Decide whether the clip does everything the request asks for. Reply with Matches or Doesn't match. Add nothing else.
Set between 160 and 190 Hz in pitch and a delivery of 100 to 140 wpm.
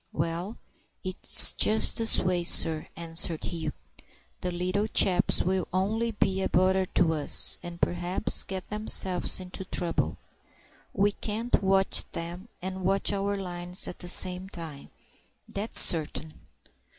Matches